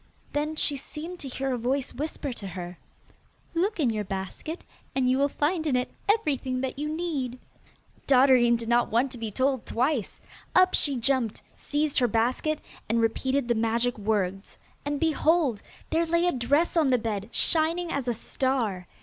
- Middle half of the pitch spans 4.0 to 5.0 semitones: Yes, average, 4.7 semitones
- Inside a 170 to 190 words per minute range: Yes, average, 175 wpm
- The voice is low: No, very high, 260 Hz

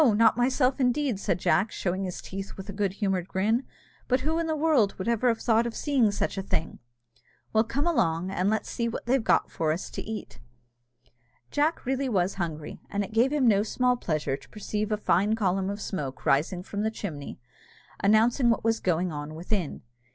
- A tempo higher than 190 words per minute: Yes, average, 200 wpm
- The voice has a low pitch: No, high, 210 Hz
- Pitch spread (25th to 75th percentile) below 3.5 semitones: No, average, 4.5 semitones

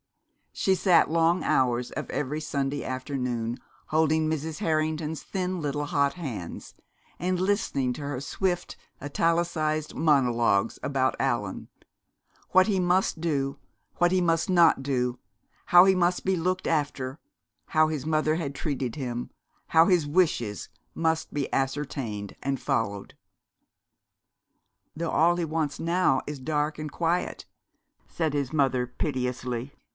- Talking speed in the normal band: No, slow, 130 wpm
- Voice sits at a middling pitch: Yes, medium, 150 Hz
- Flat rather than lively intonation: No, average, 4.0 semitones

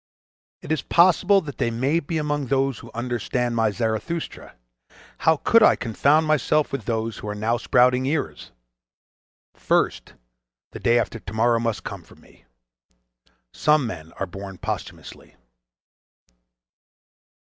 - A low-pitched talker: Yes, low, 120 Hz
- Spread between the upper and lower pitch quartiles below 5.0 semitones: No, average, 5.3 semitones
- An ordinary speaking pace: No, slow, 130 wpm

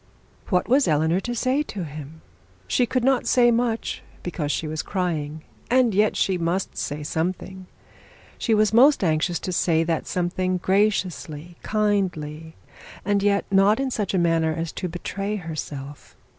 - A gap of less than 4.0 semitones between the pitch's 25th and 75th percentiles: No, average, 4.8 semitones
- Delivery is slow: No, average, 155 wpm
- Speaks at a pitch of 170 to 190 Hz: Yes, medium, 185 Hz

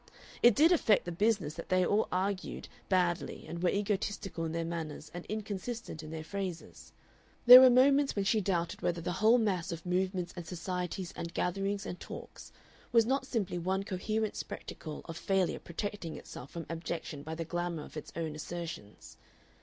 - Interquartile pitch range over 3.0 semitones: Yes, average, 3.4 semitones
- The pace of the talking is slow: No, average, 175 wpm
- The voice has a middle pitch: Yes, medium, 180 Hz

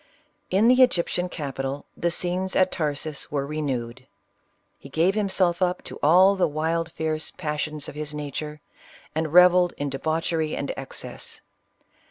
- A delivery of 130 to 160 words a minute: Yes, average, 150 wpm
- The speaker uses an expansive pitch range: No, average, 3.4 semitones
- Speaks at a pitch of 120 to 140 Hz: No, medium, 160 Hz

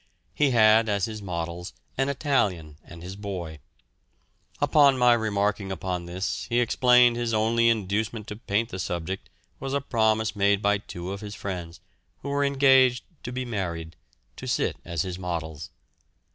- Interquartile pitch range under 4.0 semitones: No, average, 4.9 semitones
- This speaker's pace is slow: No, average, 160 wpm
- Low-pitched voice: Yes, low, 105 Hz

